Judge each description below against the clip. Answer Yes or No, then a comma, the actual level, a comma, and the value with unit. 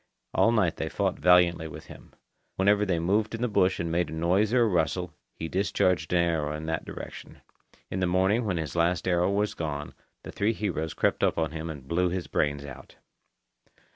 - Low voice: Yes, very low, 90 Hz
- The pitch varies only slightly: No, average, 3.2 semitones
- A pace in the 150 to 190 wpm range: No, fast, 205 wpm